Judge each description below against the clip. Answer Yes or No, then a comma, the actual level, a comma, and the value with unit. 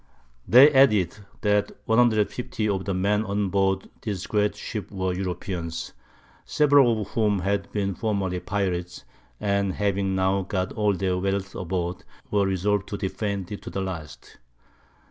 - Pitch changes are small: Yes, narrow, 1.9 semitones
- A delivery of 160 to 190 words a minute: No, average, 145 wpm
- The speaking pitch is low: Yes, low, 100 Hz